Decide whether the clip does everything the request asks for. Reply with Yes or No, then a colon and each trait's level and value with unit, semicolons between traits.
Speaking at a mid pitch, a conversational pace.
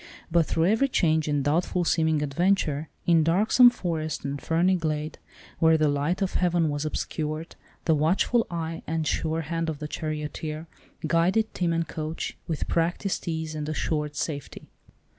Yes: medium, 160 Hz; average, 160 wpm